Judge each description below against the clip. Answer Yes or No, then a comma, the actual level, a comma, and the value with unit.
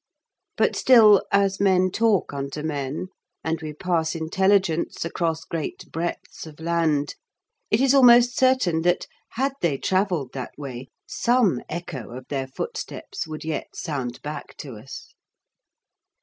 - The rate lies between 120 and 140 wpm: Yes, slow, 135 wpm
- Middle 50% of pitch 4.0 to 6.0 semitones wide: Yes, average, 5.0 semitones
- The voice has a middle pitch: Yes, medium, 165 Hz